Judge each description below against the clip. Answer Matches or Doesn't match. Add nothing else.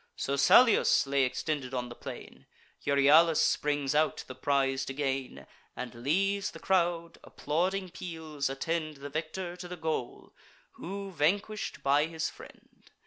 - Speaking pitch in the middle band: Matches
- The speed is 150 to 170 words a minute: Doesn't match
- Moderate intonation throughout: Matches